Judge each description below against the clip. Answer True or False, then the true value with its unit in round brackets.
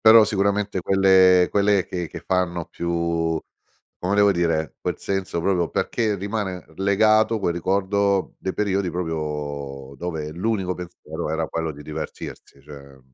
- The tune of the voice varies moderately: True (3.4 semitones)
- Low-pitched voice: True (90 Hz)